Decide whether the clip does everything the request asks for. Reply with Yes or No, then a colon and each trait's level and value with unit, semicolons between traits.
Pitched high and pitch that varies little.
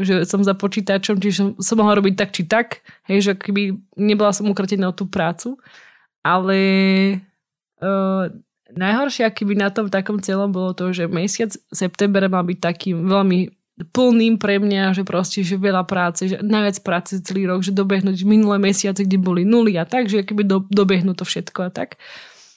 Yes: high, 195 Hz; narrow, 1.7 semitones